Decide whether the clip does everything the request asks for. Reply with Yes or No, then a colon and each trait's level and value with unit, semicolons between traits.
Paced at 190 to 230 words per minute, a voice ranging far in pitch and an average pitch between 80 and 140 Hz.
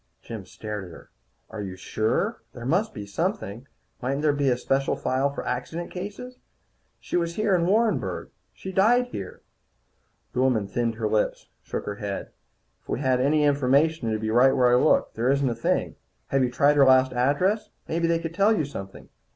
Yes: average, 195 wpm; wide, 6.3 semitones; low, 135 Hz